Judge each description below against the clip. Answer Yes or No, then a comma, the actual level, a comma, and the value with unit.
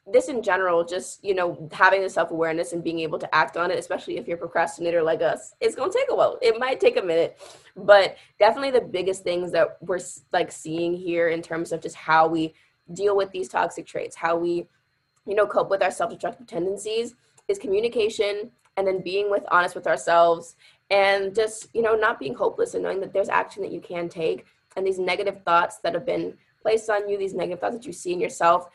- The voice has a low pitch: No, high, 190 Hz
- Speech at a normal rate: No, fast, 220 wpm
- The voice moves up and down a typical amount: Yes, average, 4.6 semitones